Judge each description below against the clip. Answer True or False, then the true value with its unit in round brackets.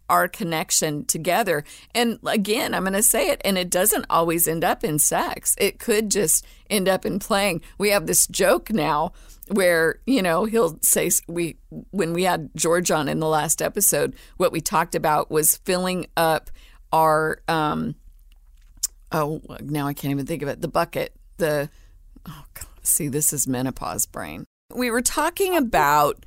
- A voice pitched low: False (165 Hz)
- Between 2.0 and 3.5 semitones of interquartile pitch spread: False (5.0 semitones)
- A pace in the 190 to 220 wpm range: False (175 wpm)